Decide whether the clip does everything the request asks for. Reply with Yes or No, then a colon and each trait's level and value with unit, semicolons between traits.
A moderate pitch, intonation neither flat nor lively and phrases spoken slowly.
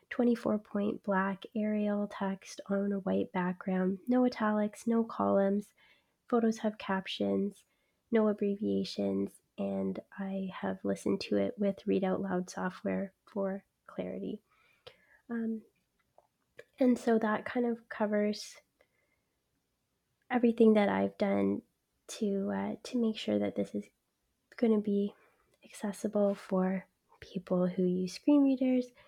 No: high, 200 Hz; average, 3.2 semitones; slow, 125 wpm